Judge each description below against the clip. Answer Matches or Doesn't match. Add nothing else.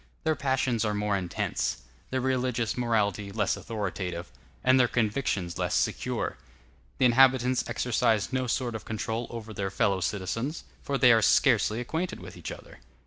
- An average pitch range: Matches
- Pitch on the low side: Matches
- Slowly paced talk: Doesn't match